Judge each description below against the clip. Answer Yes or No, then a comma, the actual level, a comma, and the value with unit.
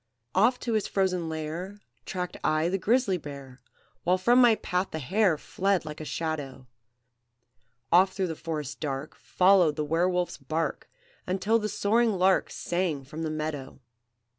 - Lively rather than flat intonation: No, average, 4.0 semitones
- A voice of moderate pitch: Yes, medium, 175 Hz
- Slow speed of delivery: No, average, 160 wpm